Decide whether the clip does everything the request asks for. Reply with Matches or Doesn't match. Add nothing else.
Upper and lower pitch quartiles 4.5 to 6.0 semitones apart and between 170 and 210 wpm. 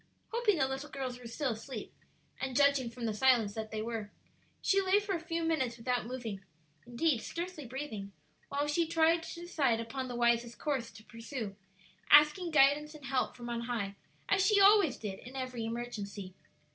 Matches